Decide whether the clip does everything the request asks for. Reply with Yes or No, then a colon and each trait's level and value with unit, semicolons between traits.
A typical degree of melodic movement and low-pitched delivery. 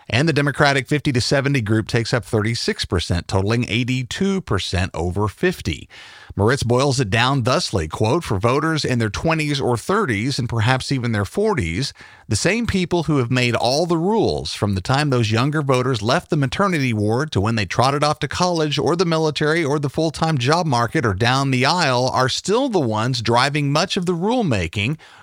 Yes: average, 5.0 semitones; low, 130 Hz